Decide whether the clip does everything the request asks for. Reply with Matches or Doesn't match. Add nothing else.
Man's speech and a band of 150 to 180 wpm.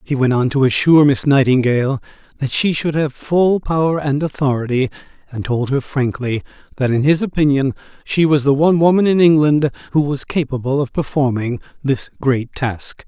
Matches